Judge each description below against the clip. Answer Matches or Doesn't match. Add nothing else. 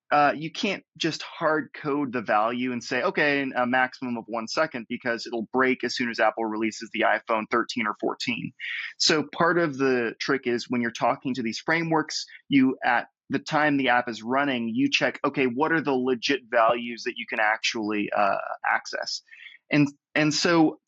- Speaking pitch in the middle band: Doesn't match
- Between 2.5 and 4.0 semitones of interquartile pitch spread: Doesn't match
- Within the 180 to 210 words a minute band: Matches